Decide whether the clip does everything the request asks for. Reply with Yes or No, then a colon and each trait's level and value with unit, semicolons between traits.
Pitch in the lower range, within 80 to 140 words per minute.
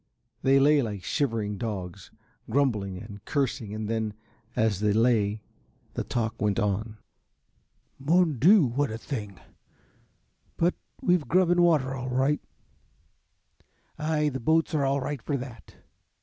Yes: low, 125 Hz; slow, 135 wpm